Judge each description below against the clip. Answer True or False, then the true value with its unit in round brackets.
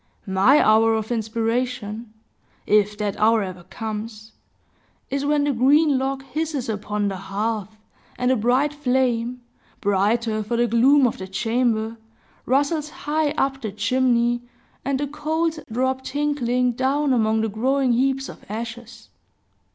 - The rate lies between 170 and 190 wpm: False (140 wpm)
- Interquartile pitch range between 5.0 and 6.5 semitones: False (3.7 semitones)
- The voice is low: False (240 Hz)